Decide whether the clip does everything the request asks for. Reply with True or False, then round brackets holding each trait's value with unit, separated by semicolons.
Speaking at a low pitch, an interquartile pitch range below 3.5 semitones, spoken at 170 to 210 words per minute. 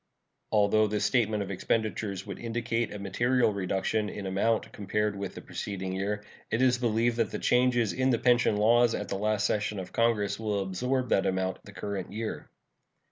True (105 Hz; 2.8 semitones; 185 wpm)